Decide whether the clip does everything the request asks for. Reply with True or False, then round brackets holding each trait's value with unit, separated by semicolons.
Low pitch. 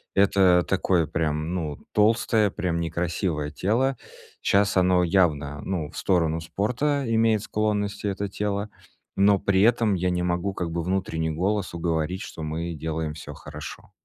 True (90 Hz)